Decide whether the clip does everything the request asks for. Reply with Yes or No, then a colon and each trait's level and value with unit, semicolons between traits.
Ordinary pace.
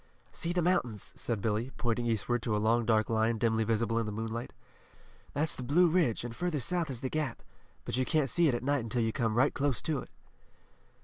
No: fast, 225 wpm